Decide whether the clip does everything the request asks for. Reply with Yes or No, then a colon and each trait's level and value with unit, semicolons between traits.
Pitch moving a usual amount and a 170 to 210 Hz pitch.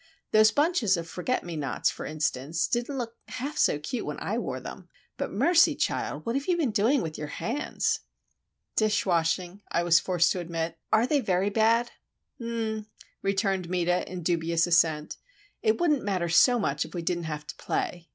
No: wide, 5.7 semitones; high, 190 Hz